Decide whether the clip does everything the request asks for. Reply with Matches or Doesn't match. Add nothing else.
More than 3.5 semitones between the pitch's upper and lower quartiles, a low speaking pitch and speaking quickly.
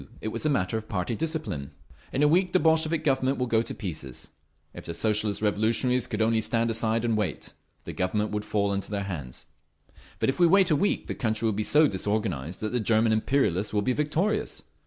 Matches